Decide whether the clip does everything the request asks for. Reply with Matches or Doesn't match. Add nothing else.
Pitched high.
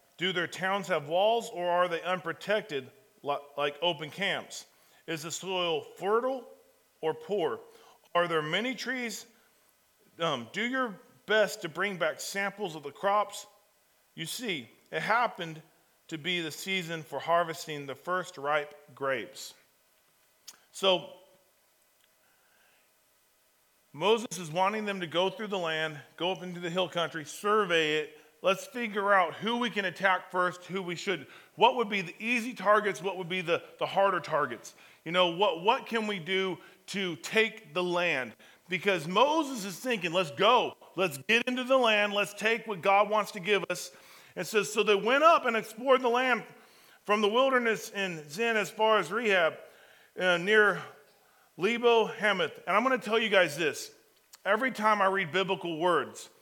Matches